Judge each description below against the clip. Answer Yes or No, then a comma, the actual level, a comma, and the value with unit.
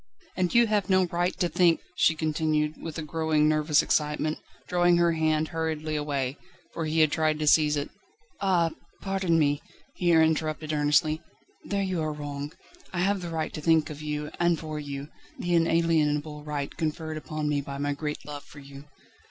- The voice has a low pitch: No, medium, 155 Hz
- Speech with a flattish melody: Yes, narrow, 2.0 semitones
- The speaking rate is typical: Yes, average, 185 wpm